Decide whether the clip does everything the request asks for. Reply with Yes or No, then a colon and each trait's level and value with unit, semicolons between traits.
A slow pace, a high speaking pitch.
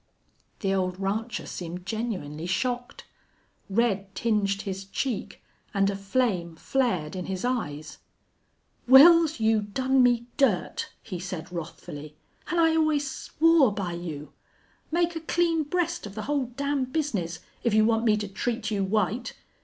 No: average, 145 wpm; high, 215 Hz